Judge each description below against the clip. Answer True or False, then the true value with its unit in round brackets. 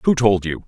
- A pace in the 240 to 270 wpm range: True (265 wpm)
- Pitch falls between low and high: False (110 Hz)